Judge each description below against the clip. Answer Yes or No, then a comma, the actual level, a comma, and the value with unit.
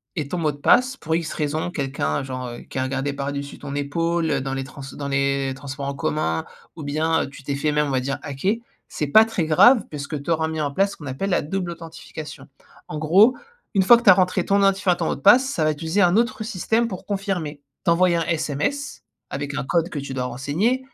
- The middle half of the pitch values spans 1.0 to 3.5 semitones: No, average, 4.8 semitones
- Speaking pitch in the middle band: Yes, medium, 155 Hz